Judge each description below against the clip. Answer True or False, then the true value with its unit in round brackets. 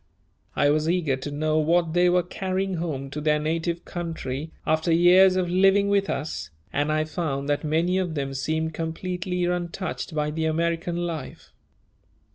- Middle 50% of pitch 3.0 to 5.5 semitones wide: False (2.6 semitones)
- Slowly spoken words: False (165 wpm)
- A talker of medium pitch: True (165 Hz)